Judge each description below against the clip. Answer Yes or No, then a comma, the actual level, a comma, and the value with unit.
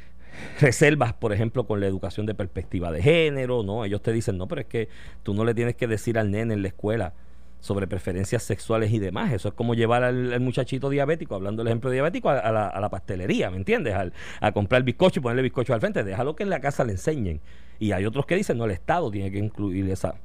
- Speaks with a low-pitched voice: Yes, low, 110 Hz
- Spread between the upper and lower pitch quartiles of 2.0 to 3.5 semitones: No, average, 4.1 semitones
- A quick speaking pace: Yes, fast, 250 wpm